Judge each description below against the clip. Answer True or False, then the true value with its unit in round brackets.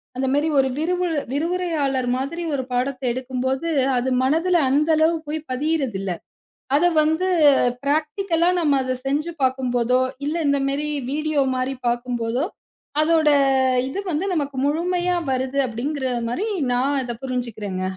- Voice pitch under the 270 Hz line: False (280 Hz)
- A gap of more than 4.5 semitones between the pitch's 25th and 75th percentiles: False (3.7 semitones)